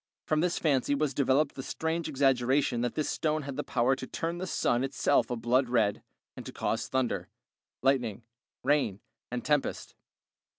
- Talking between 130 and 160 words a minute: No, average, 170 wpm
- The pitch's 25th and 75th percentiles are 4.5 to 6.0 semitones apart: No, average, 3.5 semitones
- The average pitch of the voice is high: No, low, 135 Hz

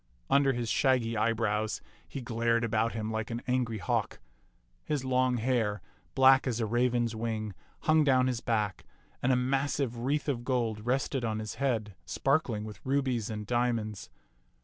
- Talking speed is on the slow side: No, average, 160 wpm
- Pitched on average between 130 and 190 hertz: No, low, 120 Hz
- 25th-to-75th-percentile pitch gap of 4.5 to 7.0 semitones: No, average, 2.8 semitones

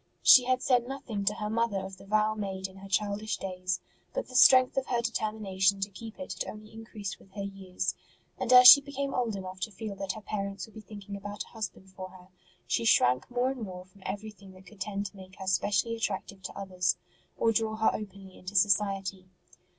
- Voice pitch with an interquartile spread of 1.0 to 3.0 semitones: Yes, narrow, 2.6 semitones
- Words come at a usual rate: No, fast, 220 wpm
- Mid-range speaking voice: No, high, 200 Hz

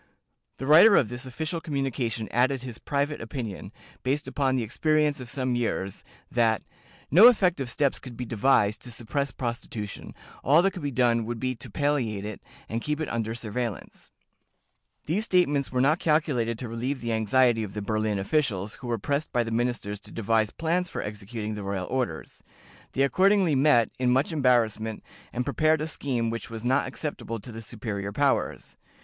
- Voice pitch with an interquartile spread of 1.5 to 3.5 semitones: No, average, 4.2 semitones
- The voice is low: Yes, low, 125 Hz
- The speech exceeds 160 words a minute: Yes, average, 180 wpm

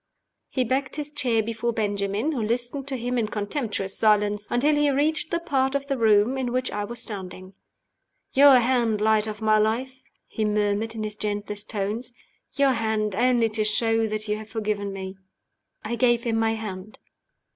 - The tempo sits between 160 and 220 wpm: Yes, average, 180 wpm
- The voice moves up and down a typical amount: Yes, average, 3.3 semitones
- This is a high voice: Yes, high, 225 Hz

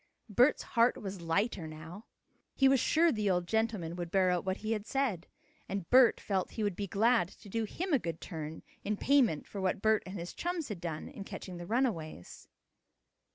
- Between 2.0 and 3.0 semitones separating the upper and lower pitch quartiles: No, average, 4.9 semitones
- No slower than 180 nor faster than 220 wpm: Yes, fast, 205 wpm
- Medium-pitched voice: No, high, 200 Hz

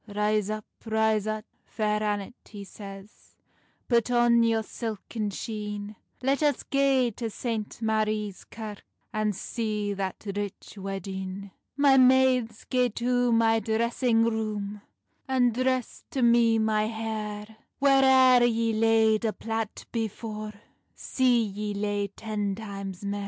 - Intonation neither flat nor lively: No, narrow, 2.2 semitones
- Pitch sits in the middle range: No, high, 220 Hz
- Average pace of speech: No, slow, 130 wpm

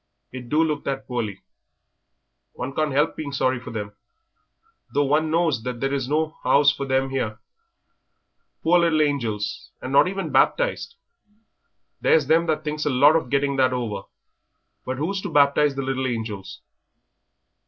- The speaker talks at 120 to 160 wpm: Yes, average, 155 wpm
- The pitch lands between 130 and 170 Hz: Yes, medium, 140 Hz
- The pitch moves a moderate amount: Yes, average, 3.3 semitones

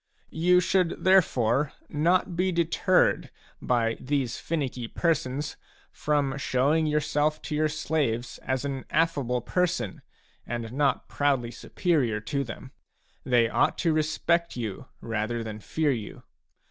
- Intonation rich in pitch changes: No, average, 4.8 semitones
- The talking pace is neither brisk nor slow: No, slow, 125 wpm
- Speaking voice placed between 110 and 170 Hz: Yes, medium, 140 Hz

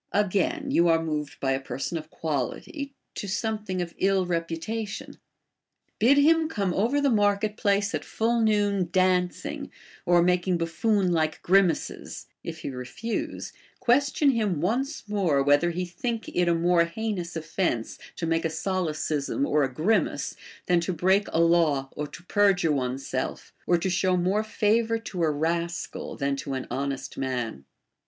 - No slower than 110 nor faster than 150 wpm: No, average, 160 wpm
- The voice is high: No, medium, 180 Hz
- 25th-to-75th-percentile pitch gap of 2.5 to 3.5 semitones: No, average, 4.6 semitones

